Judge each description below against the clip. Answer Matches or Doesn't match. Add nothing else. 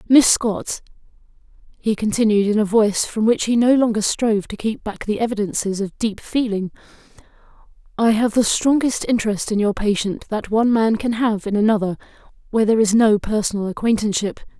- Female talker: Matches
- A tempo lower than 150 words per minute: Doesn't match